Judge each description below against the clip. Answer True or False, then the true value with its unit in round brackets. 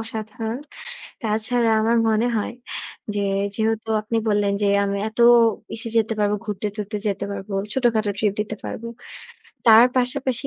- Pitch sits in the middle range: False (220 Hz)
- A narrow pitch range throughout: True (1.7 semitones)